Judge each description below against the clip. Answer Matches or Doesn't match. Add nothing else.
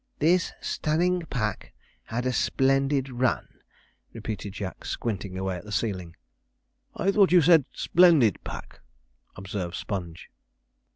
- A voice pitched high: Doesn't match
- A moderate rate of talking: Doesn't match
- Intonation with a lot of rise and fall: Matches